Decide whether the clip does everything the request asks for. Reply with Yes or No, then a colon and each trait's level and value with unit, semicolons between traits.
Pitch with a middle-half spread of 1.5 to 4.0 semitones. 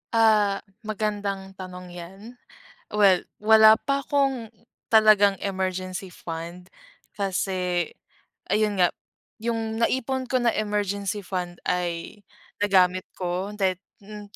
Yes: average, 2.9 semitones